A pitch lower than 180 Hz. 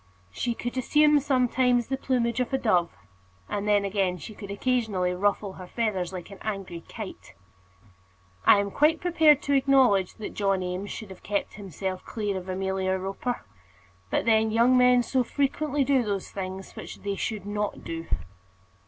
No: high, 210 Hz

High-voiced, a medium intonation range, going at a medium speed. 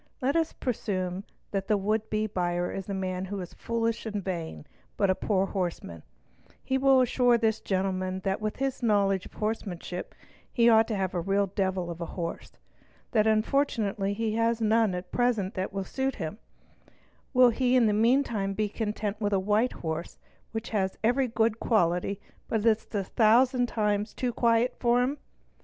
Yes: high, 210 Hz; average, 3.4 semitones; average, 185 wpm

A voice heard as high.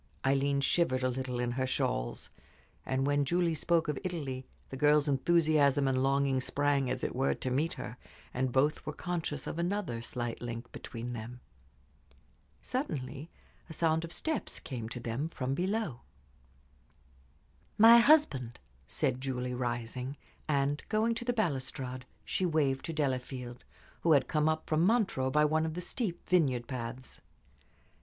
No: medium, 140 Hz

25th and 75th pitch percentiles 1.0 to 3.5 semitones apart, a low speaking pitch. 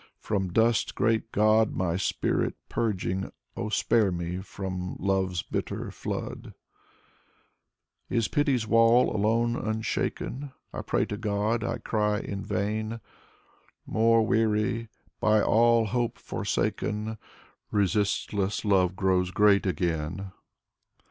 Yes: average, 2.9 semitones; low, 105 Hz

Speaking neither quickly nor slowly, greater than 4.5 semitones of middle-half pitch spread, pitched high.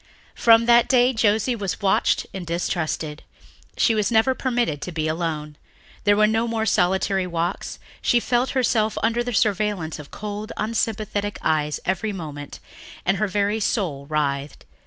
Yes: average, 155 wpm; average, 5.3 semitones; high, 205 Hz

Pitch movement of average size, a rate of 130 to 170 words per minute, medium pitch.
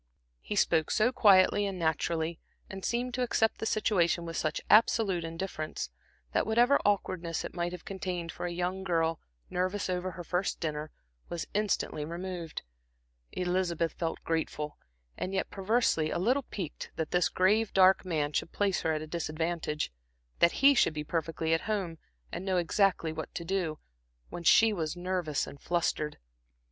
Yes: average, 3.1 semitones; average, 165 wpm; medium, 175 Hz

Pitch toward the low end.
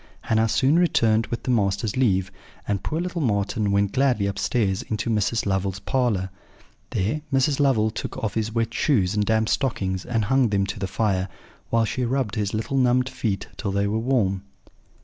Yes: low, 110 Hz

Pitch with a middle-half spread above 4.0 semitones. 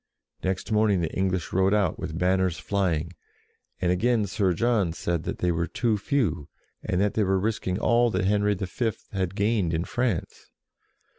No: average, 3.1 semitones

